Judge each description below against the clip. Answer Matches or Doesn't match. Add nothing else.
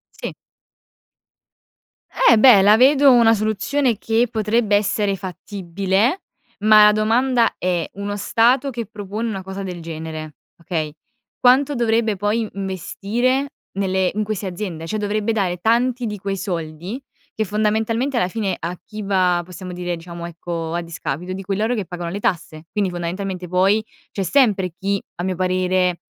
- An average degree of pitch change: Matches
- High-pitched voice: Matches